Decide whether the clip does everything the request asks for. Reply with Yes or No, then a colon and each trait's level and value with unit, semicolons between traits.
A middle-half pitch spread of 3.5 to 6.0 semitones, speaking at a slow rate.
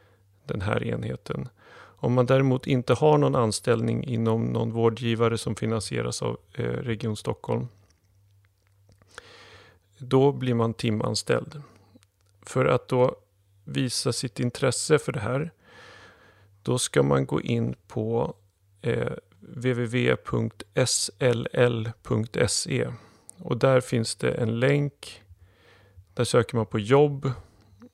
Yes: average, 4.3 semitones; slow, 105 wpm